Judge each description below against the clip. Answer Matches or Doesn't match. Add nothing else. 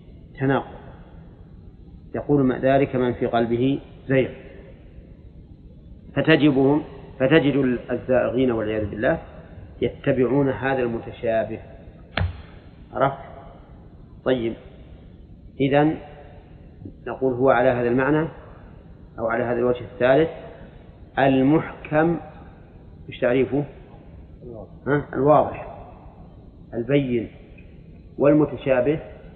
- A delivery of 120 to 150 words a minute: Doesn't match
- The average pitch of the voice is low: Matches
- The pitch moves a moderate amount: Matches